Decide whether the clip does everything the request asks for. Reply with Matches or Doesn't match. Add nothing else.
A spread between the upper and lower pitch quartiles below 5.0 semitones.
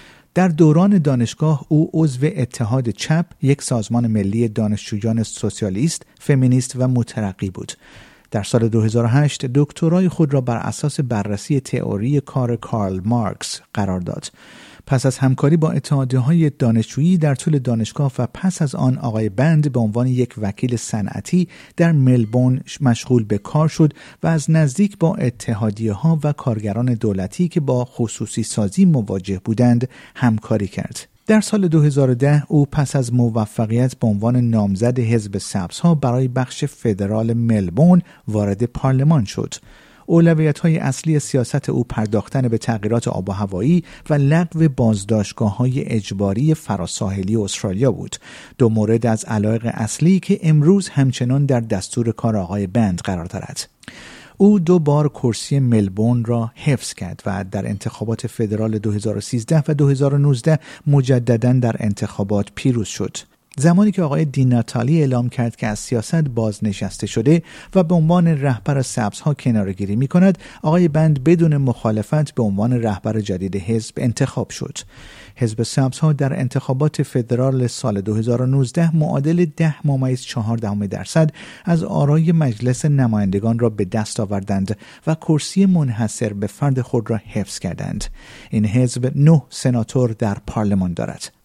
Doesn't match